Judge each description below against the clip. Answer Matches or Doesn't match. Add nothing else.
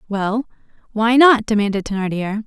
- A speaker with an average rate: Doesn't match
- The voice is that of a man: Doesn't match